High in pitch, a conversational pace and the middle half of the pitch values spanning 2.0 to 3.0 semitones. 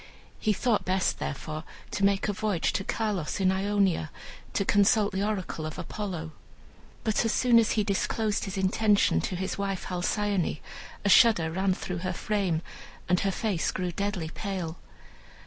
Yes: high, 195 Hz; average, 165 wpm; narrow, 2.5 semitones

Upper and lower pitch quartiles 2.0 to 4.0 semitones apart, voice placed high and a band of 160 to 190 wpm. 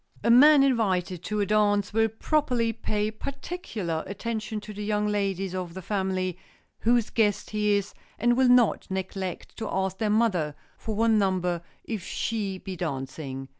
Yes: average, 3.2 semitones; high, 210 Hz; average, 165 wpm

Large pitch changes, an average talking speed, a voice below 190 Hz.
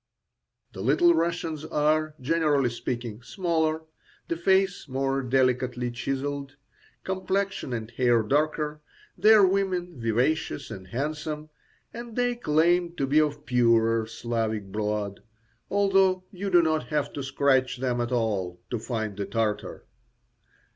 No: wide, 5.9 semitones; slow, 125 wpm; medium, 140 Hz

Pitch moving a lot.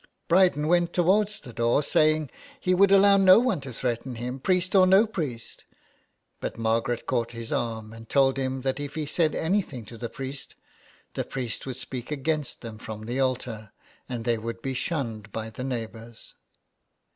Yes: wide, 5.9 semitones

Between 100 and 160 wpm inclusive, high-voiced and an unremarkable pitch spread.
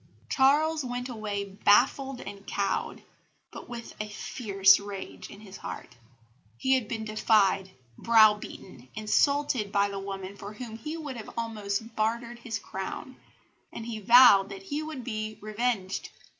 Yes: average, 145 wpm; high, 215 Hz; average, 3.5 semitones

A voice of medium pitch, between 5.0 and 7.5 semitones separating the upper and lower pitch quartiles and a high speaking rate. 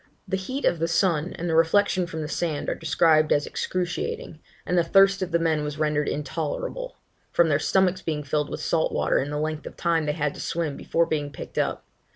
No: medium, 165 Hz; average, 3.3 semitones; fast, 220 wpm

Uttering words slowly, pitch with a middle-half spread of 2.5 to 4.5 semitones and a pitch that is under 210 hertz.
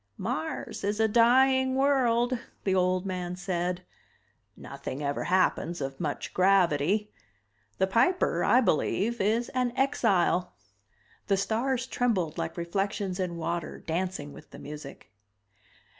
No: slow, 125 wpm; average, 5.3 semitones; high, 190 Hz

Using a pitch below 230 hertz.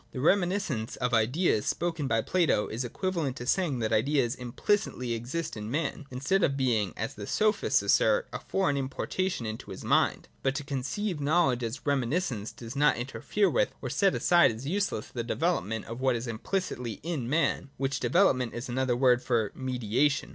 Yes: low, 135 Hz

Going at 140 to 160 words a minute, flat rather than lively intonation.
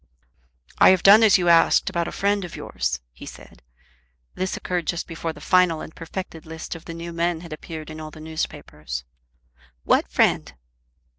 No: average, 180 wpm; narrow, 2.1 semitones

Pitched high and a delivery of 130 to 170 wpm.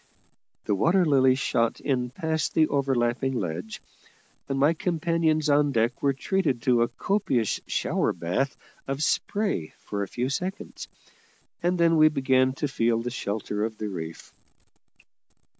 No: low, 135 Hz; average, 145 wpm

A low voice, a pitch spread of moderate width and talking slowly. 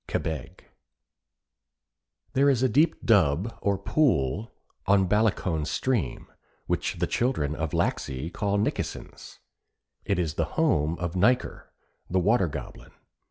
No: very low, 95 Hz; wide, 6.5 semitones; slow, 120 wpm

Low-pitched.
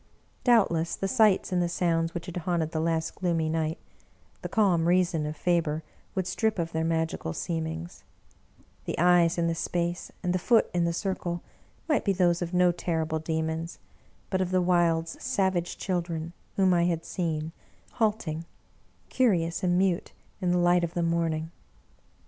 No: medium, 170 Hz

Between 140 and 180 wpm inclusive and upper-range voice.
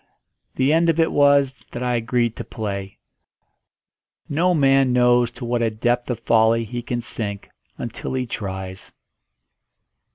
No: average, 150 wpm; low, 120 Hz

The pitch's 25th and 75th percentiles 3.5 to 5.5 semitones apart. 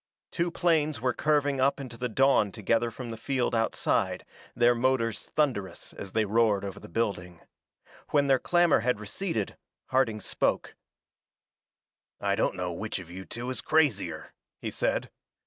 Yes: average, 4.5 semitones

